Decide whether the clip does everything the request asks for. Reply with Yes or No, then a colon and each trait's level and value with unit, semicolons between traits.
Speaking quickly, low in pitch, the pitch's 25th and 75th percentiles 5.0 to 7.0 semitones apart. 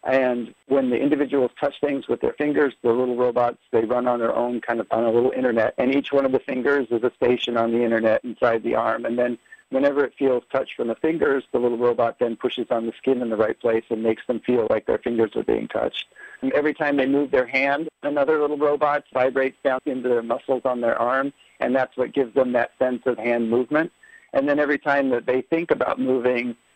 No: fast, 240 wpm; low, 130 Hz; average, 2.9 semitones